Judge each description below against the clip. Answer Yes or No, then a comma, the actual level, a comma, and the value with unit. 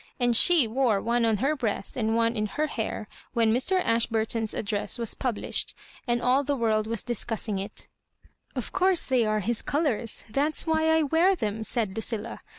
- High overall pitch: Yes, high, 235 Hz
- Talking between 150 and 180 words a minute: No, average, 195 wpm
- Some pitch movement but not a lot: Yes, average, 3.9 semitones